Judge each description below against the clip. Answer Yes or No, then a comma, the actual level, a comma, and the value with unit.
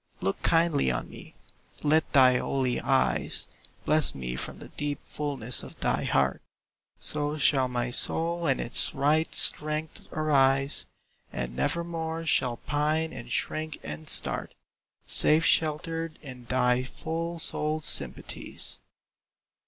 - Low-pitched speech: No, medium, 145 Hz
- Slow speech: Yes, slow, 125 wpm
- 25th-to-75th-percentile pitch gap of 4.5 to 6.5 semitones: No, average, 3.9 semitones